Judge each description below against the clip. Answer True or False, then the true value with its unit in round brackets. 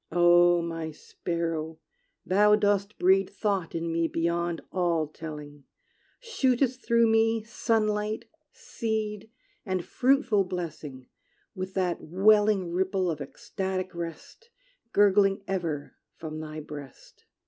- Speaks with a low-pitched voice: False (185 Hz)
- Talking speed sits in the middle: False (110 wpm)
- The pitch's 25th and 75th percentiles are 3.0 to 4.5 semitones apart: True (4.1 semitones)